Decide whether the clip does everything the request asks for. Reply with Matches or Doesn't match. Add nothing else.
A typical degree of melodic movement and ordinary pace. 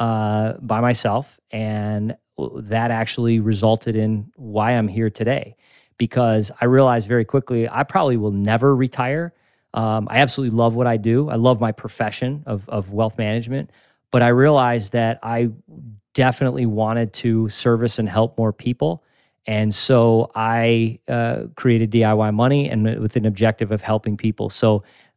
Doesn't match